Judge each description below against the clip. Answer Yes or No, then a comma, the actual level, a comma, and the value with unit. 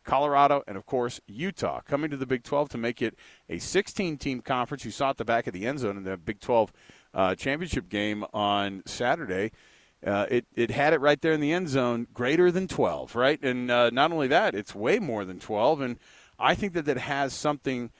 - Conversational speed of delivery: No, fast, 225 wpm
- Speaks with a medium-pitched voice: No, low, 130 Hz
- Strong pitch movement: No, average, 3.8 semitones